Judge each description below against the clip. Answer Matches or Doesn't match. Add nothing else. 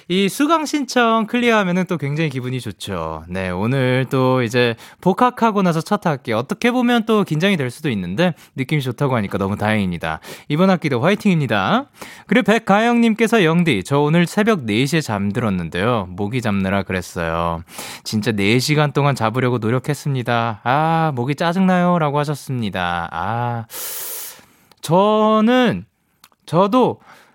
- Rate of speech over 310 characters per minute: Matches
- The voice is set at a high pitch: Doesn't match